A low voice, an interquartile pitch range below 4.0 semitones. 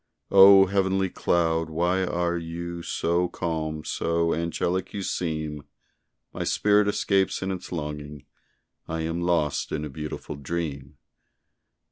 Yes: very low, 85 Hz; average, 2.9 semitones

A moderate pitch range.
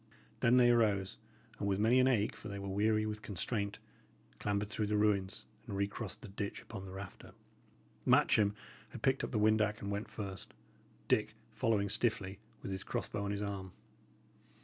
No: narrow, 1.6 semitones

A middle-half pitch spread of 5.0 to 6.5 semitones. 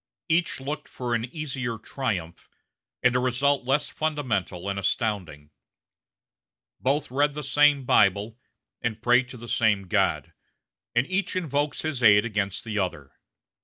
Yes: wide, 5.6 semitones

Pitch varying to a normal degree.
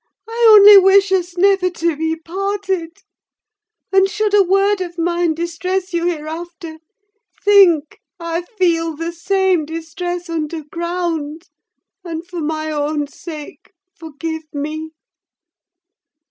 Yes: average, 3.0 semitones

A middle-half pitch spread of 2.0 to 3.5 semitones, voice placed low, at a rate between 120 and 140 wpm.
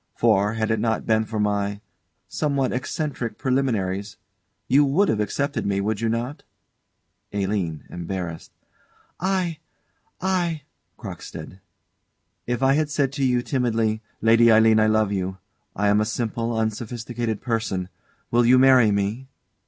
No: average, 4.1 semitones; low, 115 Hz; slow, 135 wpm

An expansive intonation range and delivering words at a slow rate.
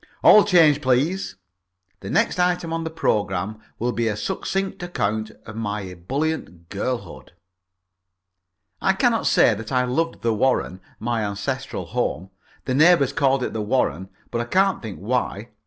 No: wide, 7.7 semitones; average, 155 wpm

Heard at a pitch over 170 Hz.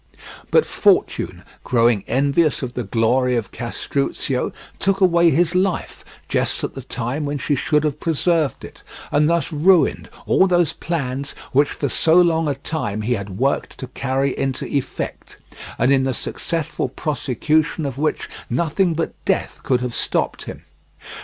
No: medium, 140 Hz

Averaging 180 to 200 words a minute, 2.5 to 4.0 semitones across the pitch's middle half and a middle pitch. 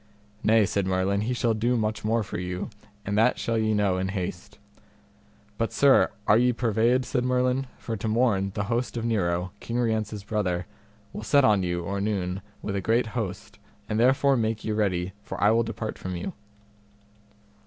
No: average, 185 wpm; average, 3.2 semitones; low, 110 Hz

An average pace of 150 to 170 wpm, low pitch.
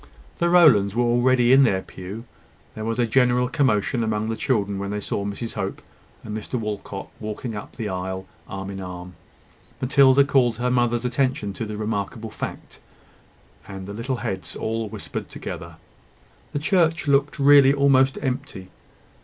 Yes: average, 160 wpm; low, 115 Hz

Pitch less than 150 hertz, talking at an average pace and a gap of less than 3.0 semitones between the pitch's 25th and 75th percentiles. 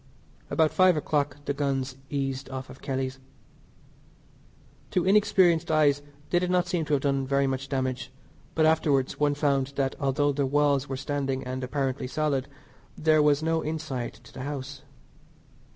Yes: medium, 140 Hz; average, 160 wpm; narrow, 2.5 semitones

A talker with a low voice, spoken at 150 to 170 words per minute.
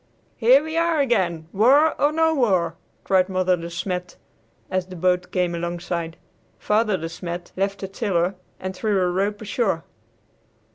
No: medium, 185 Hz; average, 155 wpm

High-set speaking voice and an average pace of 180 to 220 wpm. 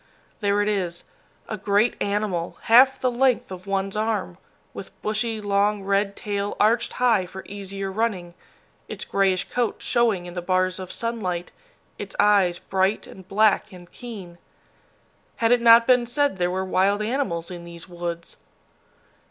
No: high, 200 Hz; average, 155 wpm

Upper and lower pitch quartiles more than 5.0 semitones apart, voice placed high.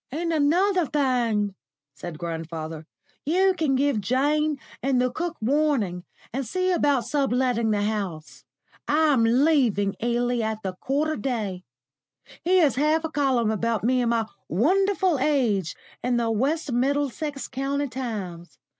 Yes: wide, 5.4 semitones; very high, 255 Hz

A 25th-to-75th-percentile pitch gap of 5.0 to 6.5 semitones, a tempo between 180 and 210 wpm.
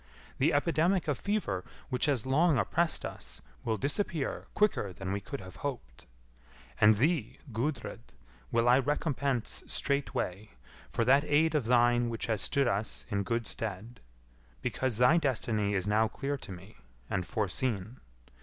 No: average, 5.3 semitones; average, 150 wpm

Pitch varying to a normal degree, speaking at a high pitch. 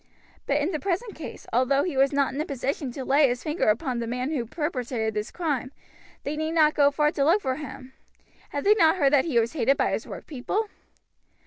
Yes: average, 3.5 semitones; very high, 280 Hz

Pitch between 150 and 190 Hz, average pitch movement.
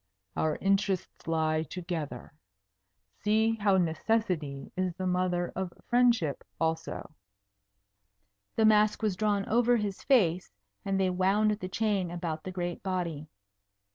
Yes: medium, 185 Hz; average, 3.9 semitones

